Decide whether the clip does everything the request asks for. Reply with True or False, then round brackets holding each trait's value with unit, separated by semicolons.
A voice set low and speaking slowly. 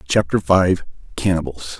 True (90 Hz; 100 wpm)